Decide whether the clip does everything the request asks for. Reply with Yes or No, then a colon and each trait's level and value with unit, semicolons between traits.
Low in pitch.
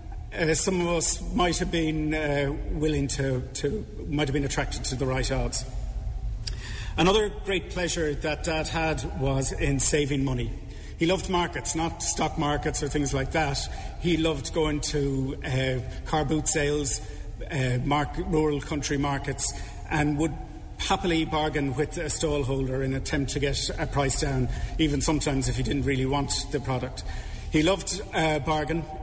No: medium, 145 Hz